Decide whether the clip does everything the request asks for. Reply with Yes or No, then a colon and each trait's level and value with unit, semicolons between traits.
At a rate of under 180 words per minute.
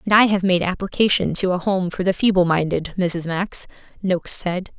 No: average, 200 wpm